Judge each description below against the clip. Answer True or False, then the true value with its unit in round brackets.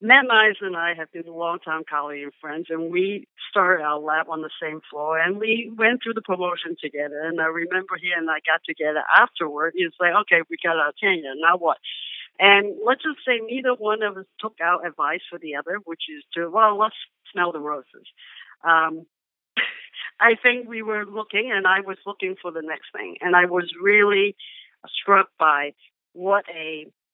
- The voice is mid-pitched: True (180 Hz)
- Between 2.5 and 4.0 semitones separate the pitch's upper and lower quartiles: False (4.4 semitones)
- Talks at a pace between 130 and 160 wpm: False (200 wpm)